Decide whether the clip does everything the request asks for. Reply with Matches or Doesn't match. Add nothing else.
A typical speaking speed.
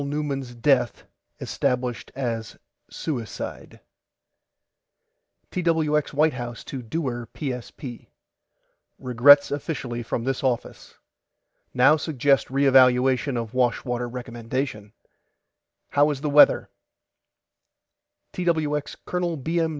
Doesn't match